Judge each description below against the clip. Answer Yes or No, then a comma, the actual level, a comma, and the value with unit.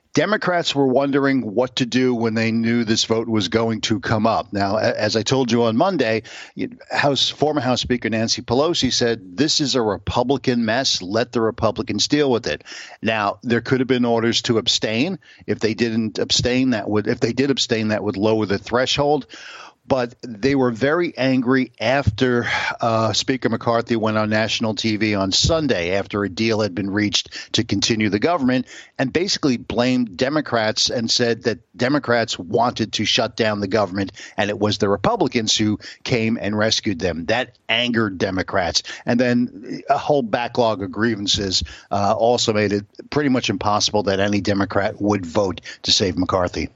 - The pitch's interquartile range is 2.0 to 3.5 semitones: Yes, average, 3.2 semitones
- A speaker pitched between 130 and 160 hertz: No, low, 115 Hz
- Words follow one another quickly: No, average, 175 wpm